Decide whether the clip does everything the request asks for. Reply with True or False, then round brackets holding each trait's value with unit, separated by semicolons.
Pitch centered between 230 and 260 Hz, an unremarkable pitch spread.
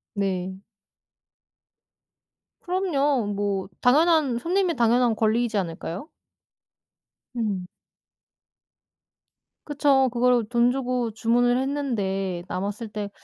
True (240 Hz; 5.0 semitones)